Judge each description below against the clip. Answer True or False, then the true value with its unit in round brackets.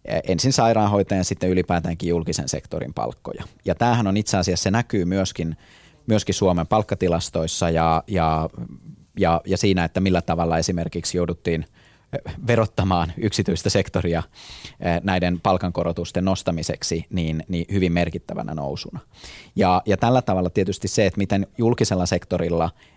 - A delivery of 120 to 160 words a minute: True (130 wpm)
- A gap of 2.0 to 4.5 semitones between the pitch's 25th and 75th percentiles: True (2.9 semitones)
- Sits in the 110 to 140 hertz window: False (90 Hz)